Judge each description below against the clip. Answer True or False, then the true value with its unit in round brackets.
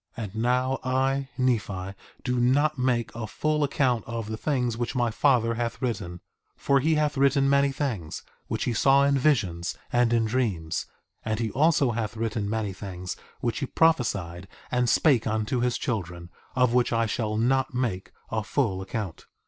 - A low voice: True (120 Hz)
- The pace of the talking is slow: False (175 wpm)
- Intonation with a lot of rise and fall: False (3.7 semitones)